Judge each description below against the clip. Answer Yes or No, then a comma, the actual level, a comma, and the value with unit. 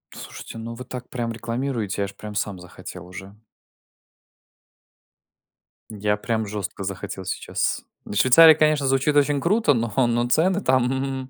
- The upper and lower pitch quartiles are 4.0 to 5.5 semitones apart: Yes, average, 4.6 semitones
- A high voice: No, low, 120 Hz